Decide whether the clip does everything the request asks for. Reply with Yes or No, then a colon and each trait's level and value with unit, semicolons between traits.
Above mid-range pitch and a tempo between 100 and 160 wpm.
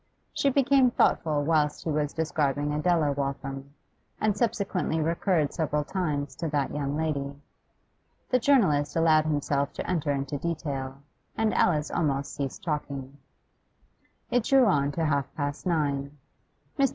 No: medium, 150 Hz; average, 140 wpm